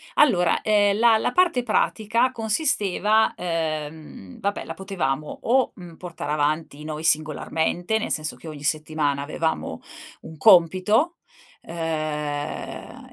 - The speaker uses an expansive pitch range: Yes, wide, 5.8 semitones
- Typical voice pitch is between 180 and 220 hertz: No, medium, 170 Hz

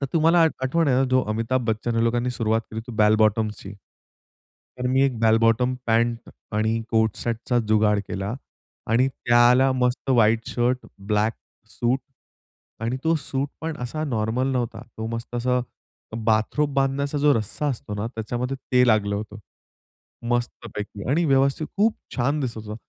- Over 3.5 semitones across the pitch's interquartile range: No, average, 3.2 semitones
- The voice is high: No, low, 120 Hz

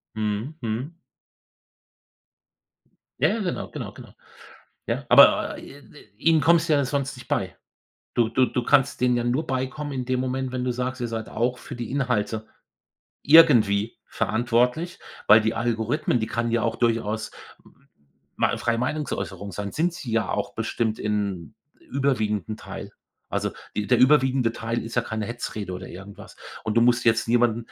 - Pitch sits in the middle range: No, low, 120 Hz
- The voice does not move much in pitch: No, average, 3.1 semitones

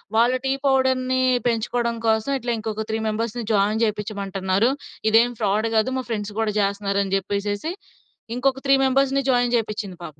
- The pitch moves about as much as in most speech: Yes, average, 3.2 semitones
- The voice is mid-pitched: No, high, 220 Hz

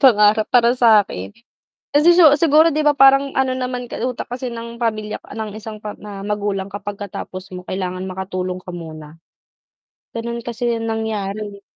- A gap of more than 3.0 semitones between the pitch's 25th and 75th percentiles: Yes, average, 3.8 semitones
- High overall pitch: Yes, high, 215 Hz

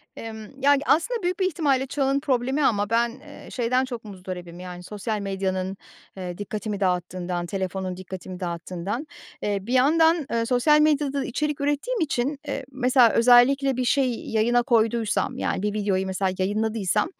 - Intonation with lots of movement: Yes, wide, 6.2 semitones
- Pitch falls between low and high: No, high, 230 Hz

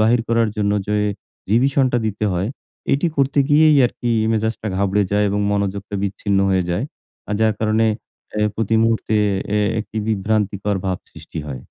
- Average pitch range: No, narrow, 2.2 semitones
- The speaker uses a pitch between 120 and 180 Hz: No, low, 110 Hz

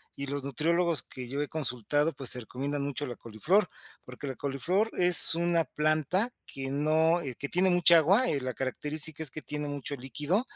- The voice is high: No, medium, 150 Hz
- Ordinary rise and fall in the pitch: Yes, average, 3.7 semitones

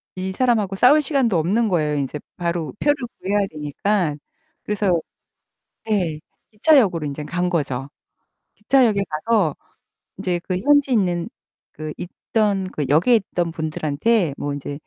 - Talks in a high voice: No, medium, 180 Hz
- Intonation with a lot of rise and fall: Yes, wide, 5.8 semitones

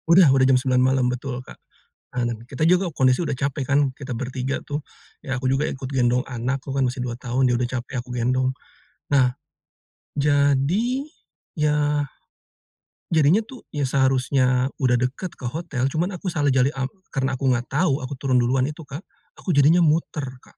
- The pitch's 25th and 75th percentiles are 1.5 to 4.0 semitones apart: Yes, narrow, 2.5 semitones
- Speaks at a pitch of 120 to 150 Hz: Yes, low, 135 Hz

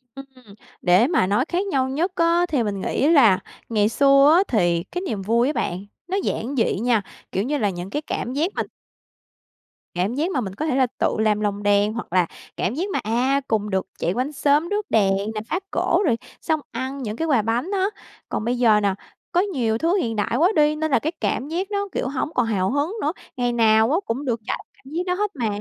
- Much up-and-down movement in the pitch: Yes, wide, 6.6 semitones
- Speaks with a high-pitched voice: Yes, very high, 255 Hz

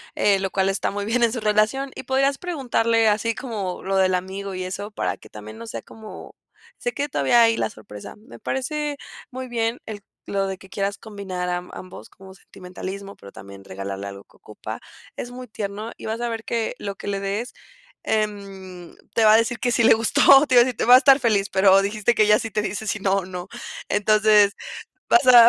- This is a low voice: No, high, 210 Hz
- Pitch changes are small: No, average, 3.4 semitones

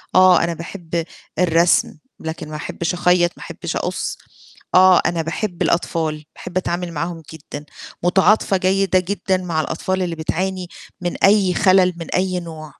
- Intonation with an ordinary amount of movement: No, narrow, 2.0 semitones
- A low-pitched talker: No, medium, 175 Hz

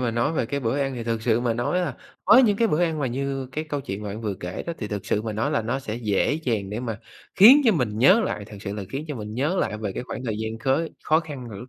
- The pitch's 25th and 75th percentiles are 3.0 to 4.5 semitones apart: No, average, 5.3 semitones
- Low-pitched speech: Yes, low, 120 Hz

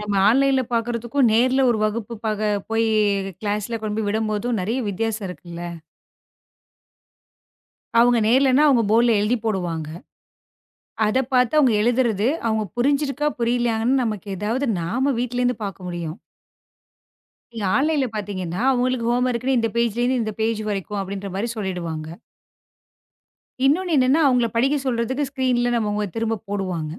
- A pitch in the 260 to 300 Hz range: No, high, 230 Hz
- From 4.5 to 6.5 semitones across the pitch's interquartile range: No, average, 3.4 semitones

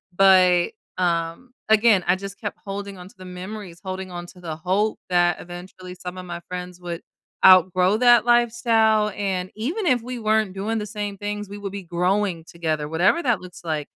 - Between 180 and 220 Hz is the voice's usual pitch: Yes, high, 190 Hz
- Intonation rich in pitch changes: No, average, 3.2 semitones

